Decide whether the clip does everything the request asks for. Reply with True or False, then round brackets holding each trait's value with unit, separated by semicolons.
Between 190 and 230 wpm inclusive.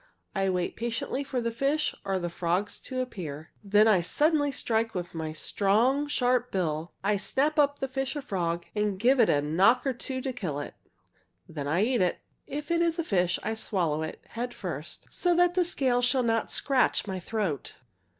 True (200 wpm)